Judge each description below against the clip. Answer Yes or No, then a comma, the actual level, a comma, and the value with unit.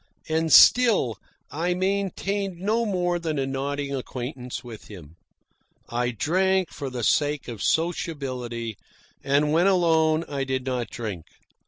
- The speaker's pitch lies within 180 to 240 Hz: No, medium, 145 Hz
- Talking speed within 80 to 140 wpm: Yes, slow, 135 wpm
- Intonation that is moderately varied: No, wide, 5.9 semitones